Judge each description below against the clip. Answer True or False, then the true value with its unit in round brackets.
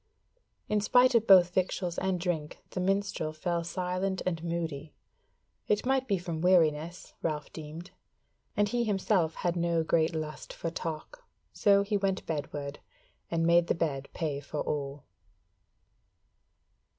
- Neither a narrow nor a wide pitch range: True (3.4 semitones)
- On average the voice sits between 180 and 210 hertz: False (170 Hz)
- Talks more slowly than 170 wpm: True (140 wpm)